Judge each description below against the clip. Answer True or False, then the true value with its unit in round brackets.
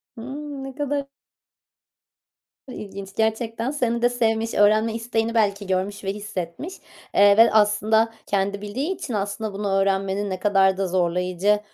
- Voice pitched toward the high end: True (210 Hz)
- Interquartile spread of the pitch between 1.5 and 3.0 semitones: True (2.7 semitones)